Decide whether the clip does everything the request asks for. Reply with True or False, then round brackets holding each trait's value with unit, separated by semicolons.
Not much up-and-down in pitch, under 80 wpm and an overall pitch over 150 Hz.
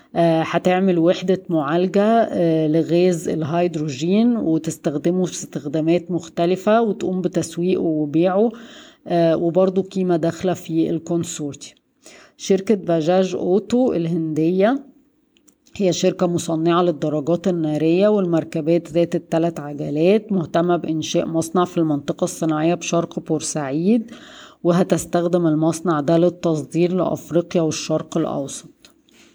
False (2.3 semitones; 90 wpm; 170 Hz)